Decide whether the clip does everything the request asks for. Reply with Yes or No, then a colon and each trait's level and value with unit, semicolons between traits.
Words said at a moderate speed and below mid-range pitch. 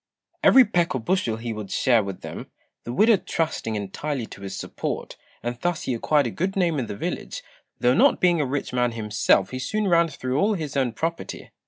No: fast, 210 wpm; low, 130 Hz